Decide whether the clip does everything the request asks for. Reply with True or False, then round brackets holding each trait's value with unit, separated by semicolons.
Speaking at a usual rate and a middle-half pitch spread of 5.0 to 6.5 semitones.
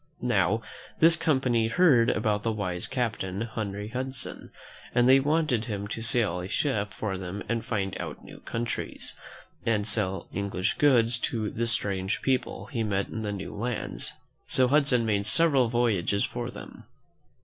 False (160 wpm; 3.5 semitones)